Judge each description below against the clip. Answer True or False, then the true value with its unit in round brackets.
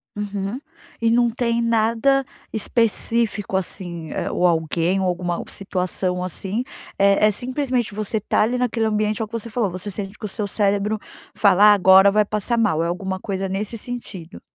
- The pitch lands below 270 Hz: True (205 Hz)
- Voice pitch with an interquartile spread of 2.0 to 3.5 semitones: True (3.2 semitones)